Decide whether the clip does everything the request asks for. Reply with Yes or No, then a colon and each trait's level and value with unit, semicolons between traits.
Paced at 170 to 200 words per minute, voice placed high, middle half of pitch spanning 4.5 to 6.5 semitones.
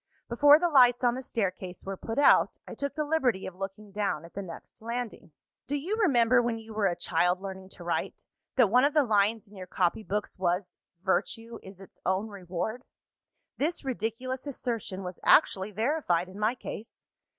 Yes: average, 190 wpm; high, 220 Hz; average, 4.8 semitones